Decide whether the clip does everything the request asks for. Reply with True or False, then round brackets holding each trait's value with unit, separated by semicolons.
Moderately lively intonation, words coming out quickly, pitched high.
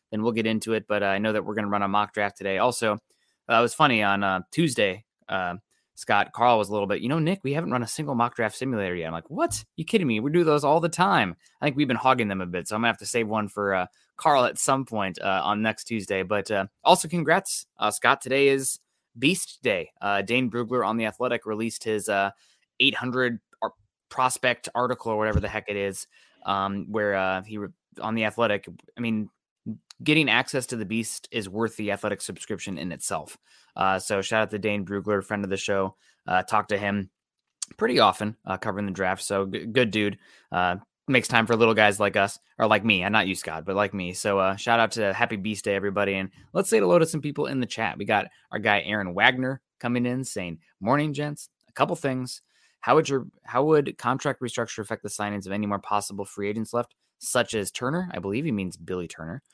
False (3.8 semitones; 240 wpm; 110 Hz)